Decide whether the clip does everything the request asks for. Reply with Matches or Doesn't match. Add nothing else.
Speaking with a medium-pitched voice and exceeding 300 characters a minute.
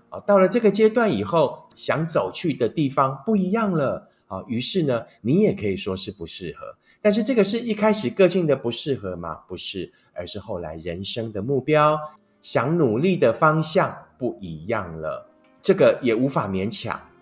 Doesn't match